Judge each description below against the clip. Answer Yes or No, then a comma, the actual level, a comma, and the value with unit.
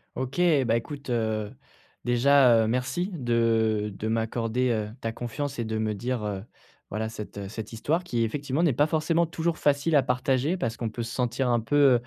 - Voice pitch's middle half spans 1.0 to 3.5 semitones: No, average, 4.1 semitones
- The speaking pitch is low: Yes, low, 120 Hz